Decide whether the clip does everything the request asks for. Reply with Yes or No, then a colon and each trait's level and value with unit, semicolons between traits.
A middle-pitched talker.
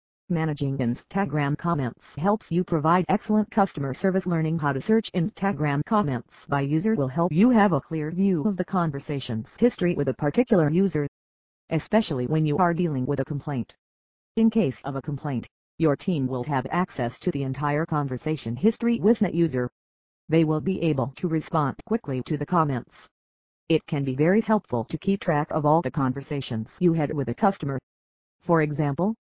Yes: medium, 155 Hz